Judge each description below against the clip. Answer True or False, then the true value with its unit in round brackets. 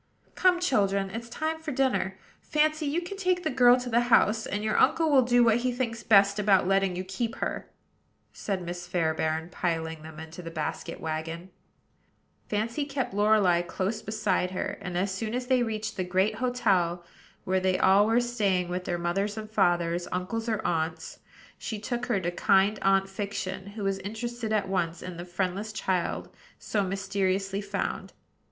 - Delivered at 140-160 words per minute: False (175 wpm)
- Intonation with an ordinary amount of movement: True (4.4 semitones)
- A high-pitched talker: True (200 Hz)